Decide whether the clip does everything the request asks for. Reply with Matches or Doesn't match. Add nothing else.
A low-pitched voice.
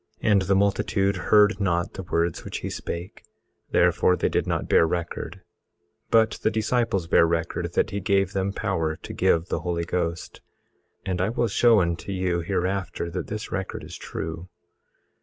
Matches